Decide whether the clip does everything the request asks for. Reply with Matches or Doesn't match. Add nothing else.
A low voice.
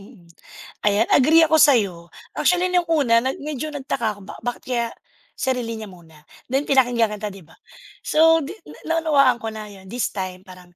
Doesn't match